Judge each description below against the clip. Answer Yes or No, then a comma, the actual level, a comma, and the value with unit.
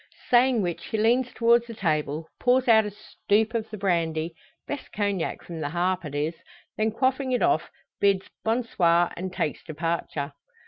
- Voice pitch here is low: No, high, 200 Hz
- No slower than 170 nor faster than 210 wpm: Yes, average, 175 wpm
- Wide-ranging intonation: Yes, wide, 5.7 semitones